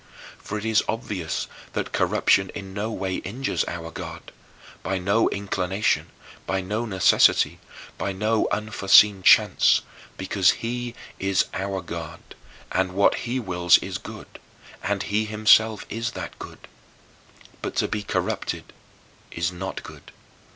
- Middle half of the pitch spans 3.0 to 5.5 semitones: No, narrow, 2.6 semitones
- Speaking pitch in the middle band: No, low, 100 Hz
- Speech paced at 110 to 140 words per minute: Yes, slow, 135 wpm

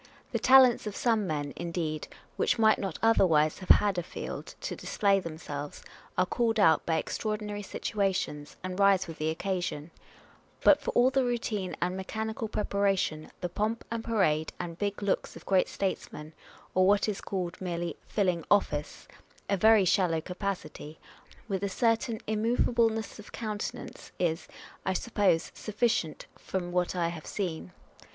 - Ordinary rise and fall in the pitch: Yes, average, 4.1 semitones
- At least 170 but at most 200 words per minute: No, average, 160 wpm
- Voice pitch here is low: No, high, 190 Hz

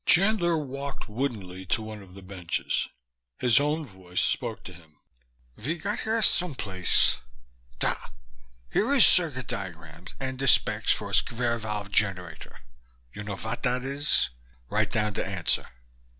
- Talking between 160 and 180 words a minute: No, average, 150 wpm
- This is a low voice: Yes, low, 115 Hz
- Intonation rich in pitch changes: Yes, wide, 6.6 semitones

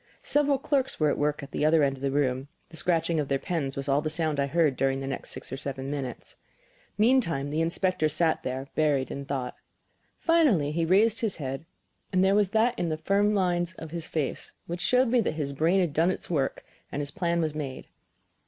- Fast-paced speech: Yes, fast, 225 wpm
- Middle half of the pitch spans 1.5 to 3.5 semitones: No, average, 4.8 semitones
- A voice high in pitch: No, medium, 155 Hz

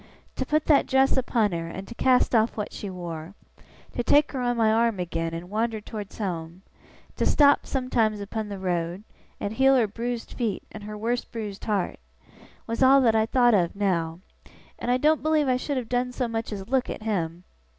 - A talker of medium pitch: No, high, 220 Hz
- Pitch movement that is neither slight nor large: Yes, average, 4.5 semitones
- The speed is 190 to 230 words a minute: Yes, average, 200 wpm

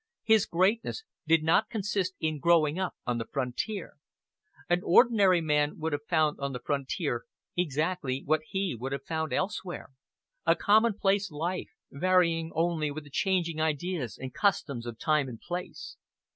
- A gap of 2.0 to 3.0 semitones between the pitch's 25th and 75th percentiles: No, average, 4.1 semitones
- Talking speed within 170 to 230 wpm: No, average, 155 wpm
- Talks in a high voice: No, medium, 165 Hz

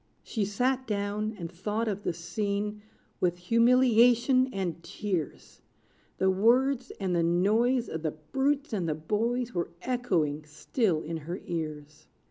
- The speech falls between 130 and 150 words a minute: Yes, average, 140 wpm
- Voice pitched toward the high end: Yes, high, 205 Hz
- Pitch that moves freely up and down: Yes, wide, 5.9 semitones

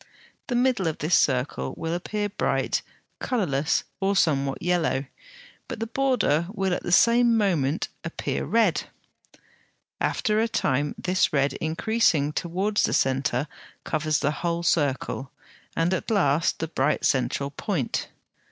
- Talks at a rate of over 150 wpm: No, slow, 135 wpm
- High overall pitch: No, medium, 170 Hz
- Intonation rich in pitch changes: Yes, wide, 6.1 semitones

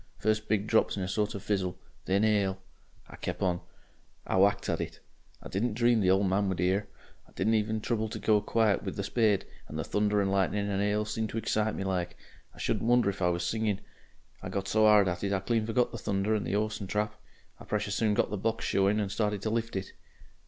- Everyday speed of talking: No, fast, 235 wpm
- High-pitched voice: No, low, 105 Hz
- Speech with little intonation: Yes, narrow, 1.9 semitones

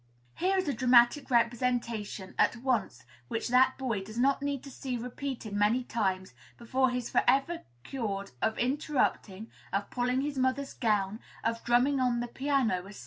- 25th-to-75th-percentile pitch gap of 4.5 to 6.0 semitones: No, average, 3.2 semitones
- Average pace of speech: Yes, average, 165 wpm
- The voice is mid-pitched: No, high, 245 Hz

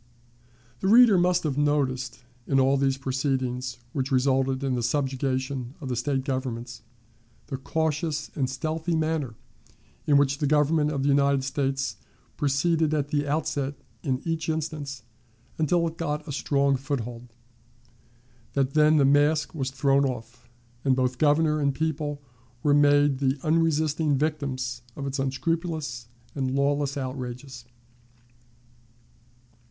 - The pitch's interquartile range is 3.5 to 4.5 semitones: No, narrow, 2.5 semitones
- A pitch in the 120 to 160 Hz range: Yes, medium, 140 Hz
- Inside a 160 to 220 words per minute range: No, slow, 135 wpm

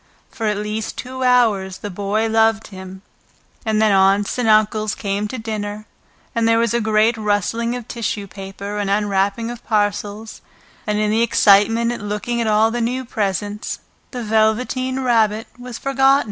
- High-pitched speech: Yes, high, 215 Hz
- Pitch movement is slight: Yes, narrow, 2.2 semitones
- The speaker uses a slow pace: No, average, 170 wpm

